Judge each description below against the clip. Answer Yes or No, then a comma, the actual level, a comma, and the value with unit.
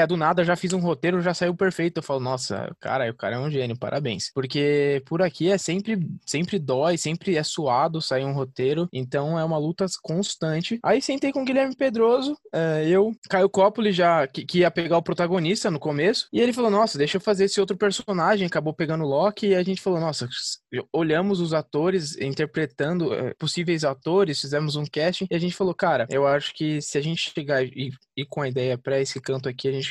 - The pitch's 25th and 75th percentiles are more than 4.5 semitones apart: Yes, average, 4.9 semitones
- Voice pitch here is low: No, medium, 165 Hz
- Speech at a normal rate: No, fast, 210 wpm